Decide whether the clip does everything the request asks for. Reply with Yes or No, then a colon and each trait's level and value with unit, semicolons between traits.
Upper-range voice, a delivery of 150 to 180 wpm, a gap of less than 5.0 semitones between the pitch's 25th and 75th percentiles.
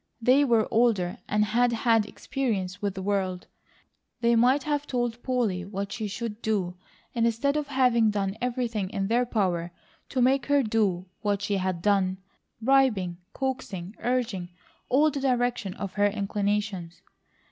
Yes: high, 220 Hz; average, 155 wpm; average, 4.1 semitones